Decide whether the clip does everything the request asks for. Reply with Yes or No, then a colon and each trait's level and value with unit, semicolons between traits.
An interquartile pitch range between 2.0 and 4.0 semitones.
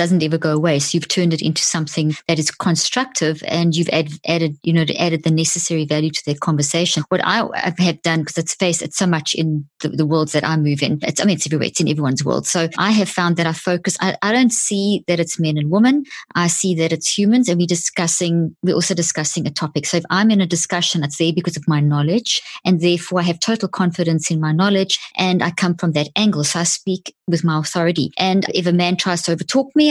Yes: narrow, 2.5 semitones